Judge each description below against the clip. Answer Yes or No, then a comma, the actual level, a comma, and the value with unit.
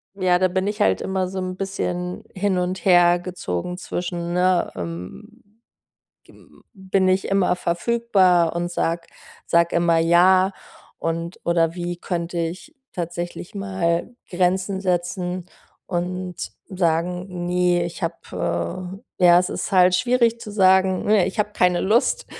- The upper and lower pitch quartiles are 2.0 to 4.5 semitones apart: No, narrow, 1.6 semitones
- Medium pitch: Yes, medium, 180 Hz